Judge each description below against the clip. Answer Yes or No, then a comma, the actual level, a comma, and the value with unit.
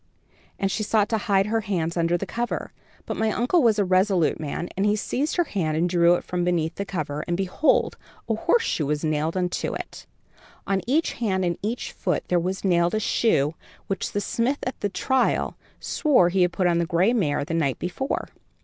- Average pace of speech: No, fast, 210 wpm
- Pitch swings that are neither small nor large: Yes, average, 4.1 semitones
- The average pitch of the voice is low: No, high, 190 Hz